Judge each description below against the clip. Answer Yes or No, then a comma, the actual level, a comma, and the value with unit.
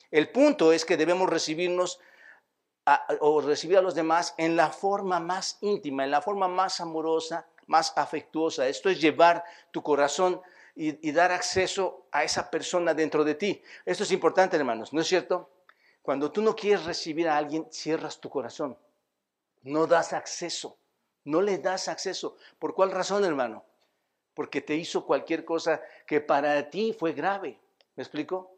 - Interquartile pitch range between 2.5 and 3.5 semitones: Yes, average, 3.0 semitones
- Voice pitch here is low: No, medium, 170 Hz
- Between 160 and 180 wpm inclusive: Yes, average, 165 wpm